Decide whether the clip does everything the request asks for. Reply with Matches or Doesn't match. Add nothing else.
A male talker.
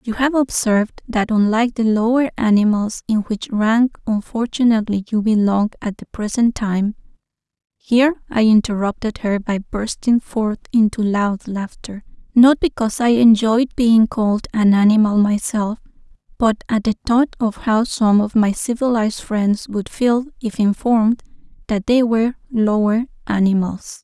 Doesn't match